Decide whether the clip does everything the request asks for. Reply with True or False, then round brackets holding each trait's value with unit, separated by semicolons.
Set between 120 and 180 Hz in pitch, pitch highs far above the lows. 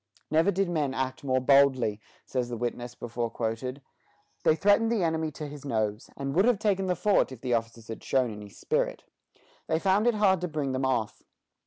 True (135 Hz; 6.5 semitones)